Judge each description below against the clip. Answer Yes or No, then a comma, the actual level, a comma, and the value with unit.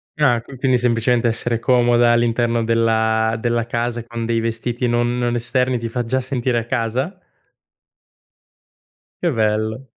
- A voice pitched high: No, low, 120 Hz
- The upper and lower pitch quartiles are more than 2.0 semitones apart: No, narrow, 1.3 semitones